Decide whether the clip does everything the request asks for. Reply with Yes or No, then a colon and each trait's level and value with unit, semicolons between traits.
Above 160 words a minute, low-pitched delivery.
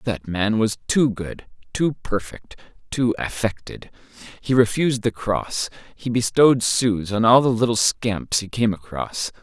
No: average, 155 wpm; low, 110 Hz